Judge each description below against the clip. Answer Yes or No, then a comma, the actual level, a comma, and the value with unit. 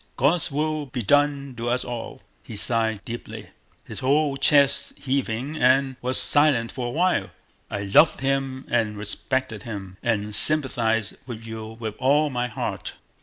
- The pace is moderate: Yes, average, 155 wpm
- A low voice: Yes, low, 125 Hz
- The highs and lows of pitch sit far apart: No, average, 3.9 semitones